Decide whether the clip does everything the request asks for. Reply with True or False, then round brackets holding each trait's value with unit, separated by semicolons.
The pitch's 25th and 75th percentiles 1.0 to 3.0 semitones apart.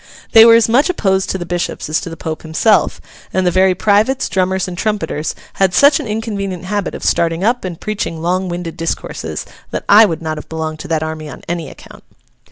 False (4.2 semitones)